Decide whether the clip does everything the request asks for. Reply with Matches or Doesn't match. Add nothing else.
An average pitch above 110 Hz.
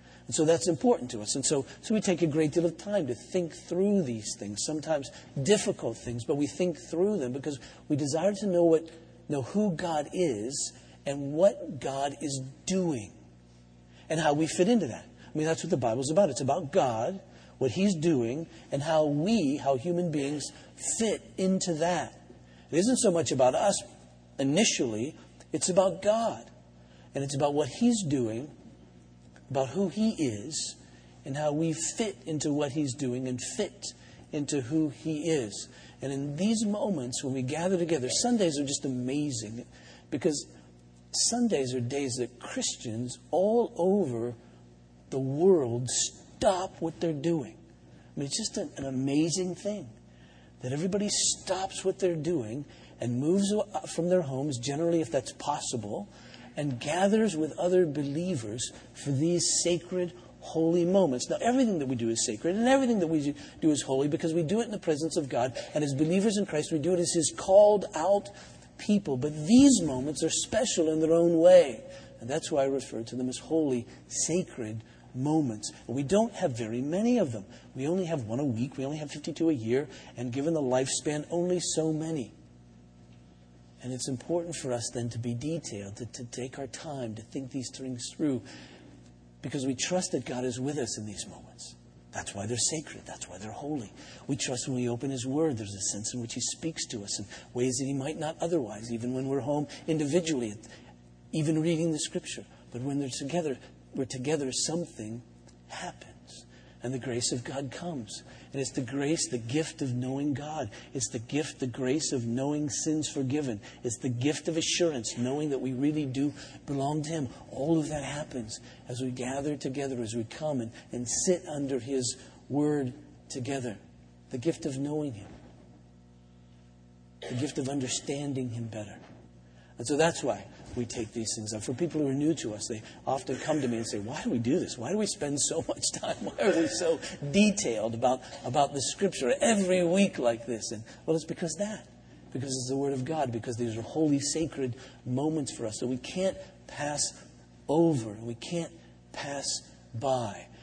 Matches